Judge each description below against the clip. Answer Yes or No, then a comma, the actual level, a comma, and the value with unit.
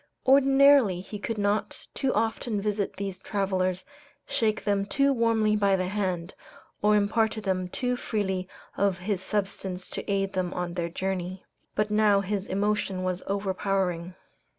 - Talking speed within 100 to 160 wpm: Yes, average, 150 wpm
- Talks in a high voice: Yes, high, 200 Hz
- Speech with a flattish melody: Yes, narrow, 2.3 semitones